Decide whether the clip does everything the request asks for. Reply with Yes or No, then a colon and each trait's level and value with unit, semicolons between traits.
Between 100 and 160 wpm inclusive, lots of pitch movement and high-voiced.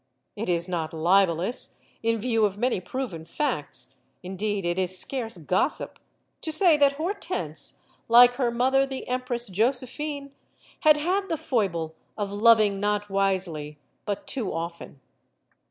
Yes: average, 140 wpm; wide, 6.6 semitones; high, 215 Hz